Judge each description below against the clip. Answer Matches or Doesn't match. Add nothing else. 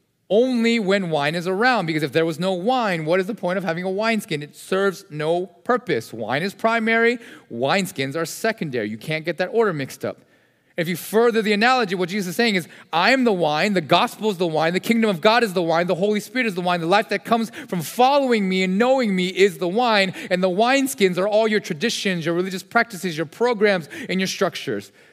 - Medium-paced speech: Doesn't match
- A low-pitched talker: Doesn't match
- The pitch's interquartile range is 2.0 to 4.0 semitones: Doesn't match